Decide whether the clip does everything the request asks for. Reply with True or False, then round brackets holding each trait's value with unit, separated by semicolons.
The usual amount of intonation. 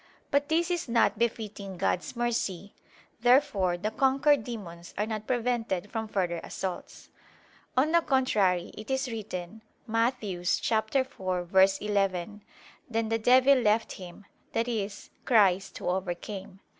True (4.4 semitones)